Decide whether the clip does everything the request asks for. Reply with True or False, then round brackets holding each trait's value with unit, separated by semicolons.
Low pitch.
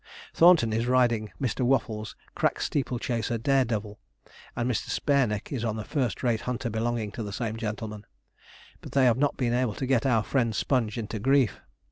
True (120 Hz)